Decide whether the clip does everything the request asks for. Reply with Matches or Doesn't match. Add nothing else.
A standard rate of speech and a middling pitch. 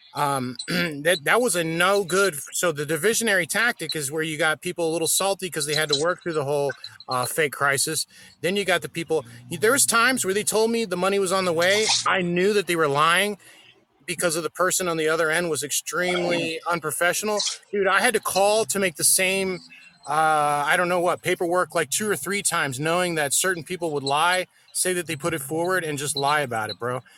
Doesn't match